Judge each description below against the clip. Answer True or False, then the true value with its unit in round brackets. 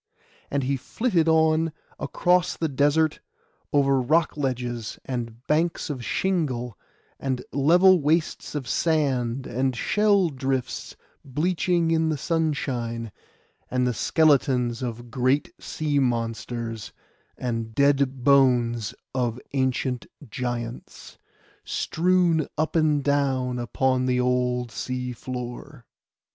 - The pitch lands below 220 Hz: True (135 Hz)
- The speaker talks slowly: True (110 wpm)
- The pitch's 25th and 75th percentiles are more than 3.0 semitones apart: True (4.1 semitones)